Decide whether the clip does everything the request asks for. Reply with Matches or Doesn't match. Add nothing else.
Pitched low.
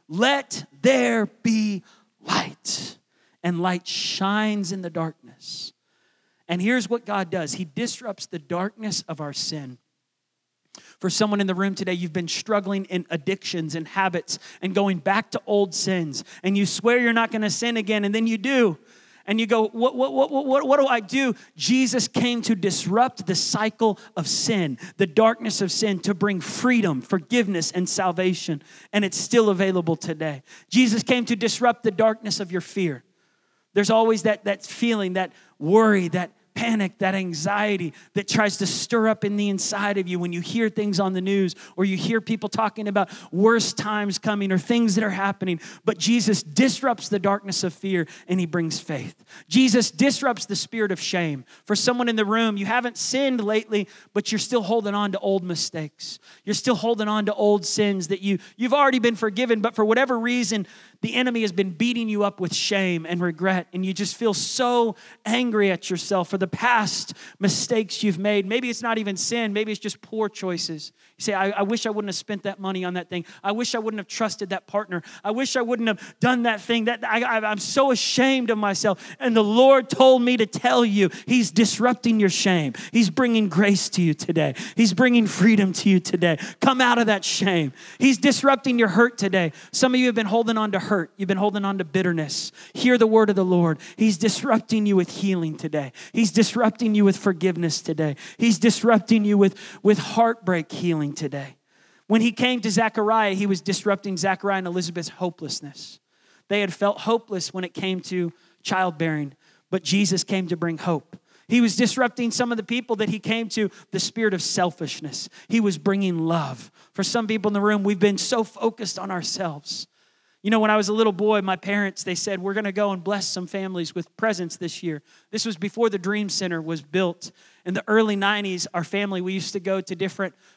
Doesn't match